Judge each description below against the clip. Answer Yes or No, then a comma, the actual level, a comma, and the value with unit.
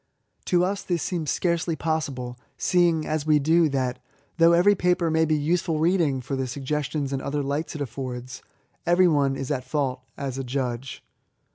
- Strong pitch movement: No, average, 4.0 semitones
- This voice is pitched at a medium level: Yes, medium, 150 Hz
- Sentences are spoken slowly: No, average, 180 wpm